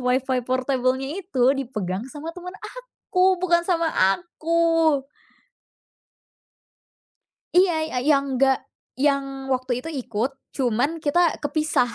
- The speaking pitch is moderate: No, very high, 280 Hz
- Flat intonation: No, average, 4.5 semitones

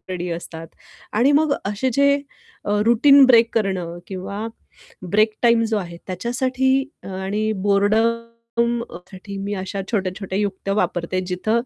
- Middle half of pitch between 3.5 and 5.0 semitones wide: Yes, average, 3.8 semitones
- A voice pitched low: No, high, 205 Hz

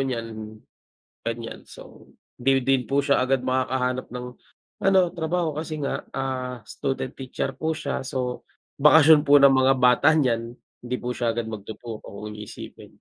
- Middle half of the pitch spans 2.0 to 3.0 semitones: Yes, narrow, 2.4 semitones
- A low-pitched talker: Yes, low, 130 Hz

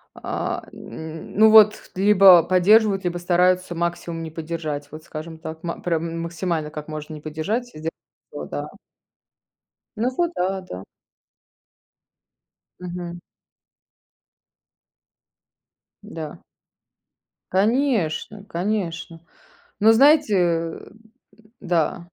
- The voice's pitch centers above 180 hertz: No, medium, 175 Hz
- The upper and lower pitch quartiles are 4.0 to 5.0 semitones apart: No, average, 3.6 semitones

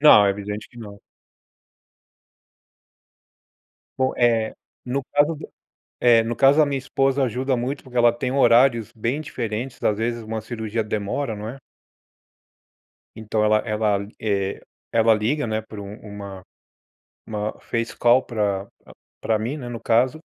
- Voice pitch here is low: Yes, low, 115 Hz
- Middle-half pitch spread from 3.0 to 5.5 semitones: Yes, average, 3.3 semitones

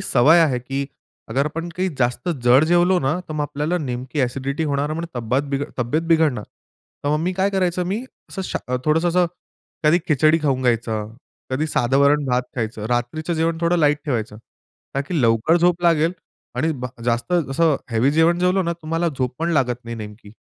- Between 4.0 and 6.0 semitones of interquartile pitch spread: Yes, average, 5.1 semitones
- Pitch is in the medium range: Yes, medium, 145 Hz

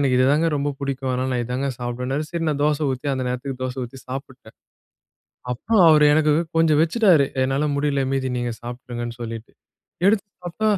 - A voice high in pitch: No, low, 135 Hz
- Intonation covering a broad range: No, average, 3.2 semitones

